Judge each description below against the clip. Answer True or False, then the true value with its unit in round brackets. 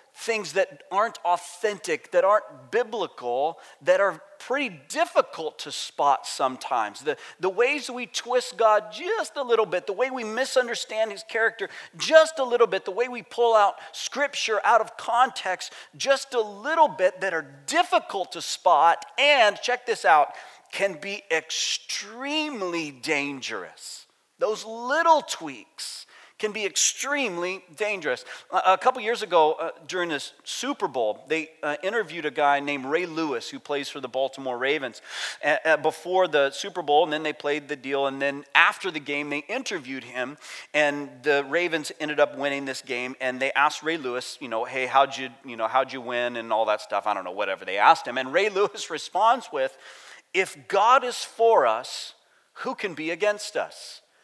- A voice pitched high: True (195 Hz)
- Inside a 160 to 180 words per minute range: True (170 wpm)